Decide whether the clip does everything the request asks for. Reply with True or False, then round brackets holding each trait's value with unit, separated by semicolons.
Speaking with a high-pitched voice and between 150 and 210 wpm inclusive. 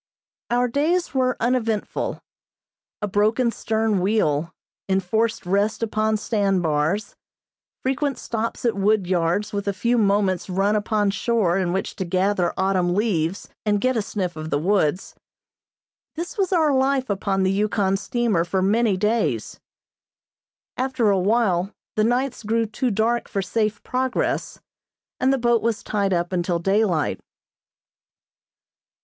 False (210 Hz; 140 wpm)